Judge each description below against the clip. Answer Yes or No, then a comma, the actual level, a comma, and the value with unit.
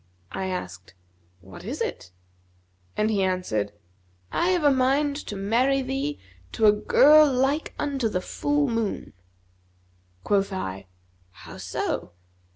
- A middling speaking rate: No, slow, 125 wpm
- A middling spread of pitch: No, wide, 7.1 semitones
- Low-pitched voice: No, high, 225 Hz